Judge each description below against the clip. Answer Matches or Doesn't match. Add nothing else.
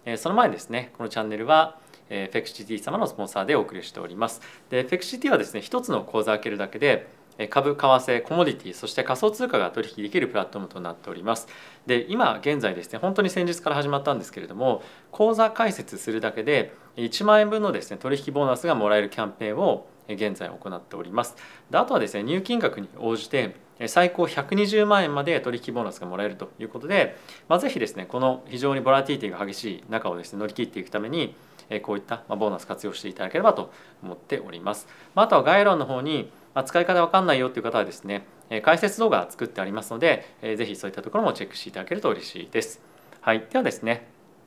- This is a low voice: Matches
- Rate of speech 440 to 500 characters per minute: Matches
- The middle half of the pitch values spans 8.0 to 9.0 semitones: Matches